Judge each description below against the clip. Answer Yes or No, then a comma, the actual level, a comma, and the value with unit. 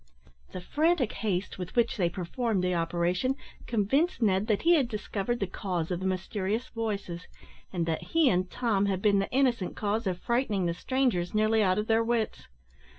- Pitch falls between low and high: No, high, 205 Hz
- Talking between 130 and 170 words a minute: No, average, 185 wpm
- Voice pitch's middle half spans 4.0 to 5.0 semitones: Yes, average, 4.4 semitones